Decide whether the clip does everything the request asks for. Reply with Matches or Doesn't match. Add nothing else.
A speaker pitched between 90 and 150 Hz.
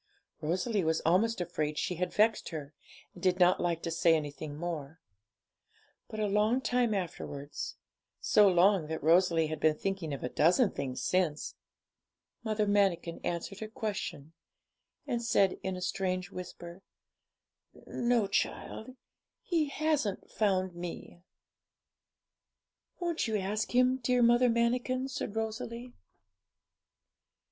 Doesn't match